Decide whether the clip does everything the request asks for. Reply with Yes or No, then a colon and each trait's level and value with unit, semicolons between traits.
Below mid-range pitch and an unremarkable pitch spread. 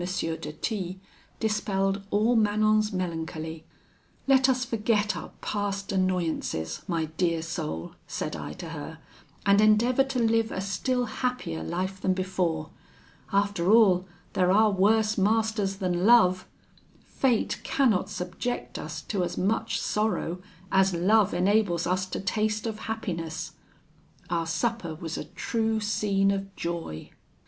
No: high, 195 Hz; average, 3.7 semitones